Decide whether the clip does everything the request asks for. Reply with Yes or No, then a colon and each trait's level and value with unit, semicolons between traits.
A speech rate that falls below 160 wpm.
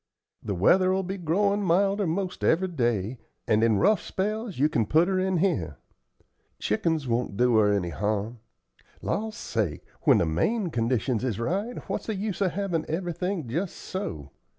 No: average, 165 wpm